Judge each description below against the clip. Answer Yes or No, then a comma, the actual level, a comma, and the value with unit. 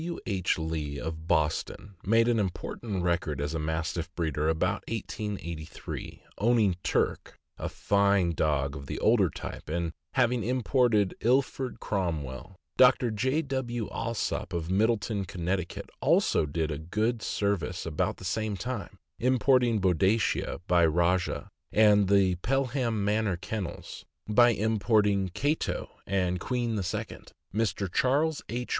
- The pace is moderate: No, slow, 130 wpm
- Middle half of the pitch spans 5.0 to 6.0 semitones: Yes, average, 5.3 semitones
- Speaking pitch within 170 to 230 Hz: No, low, 100 Hz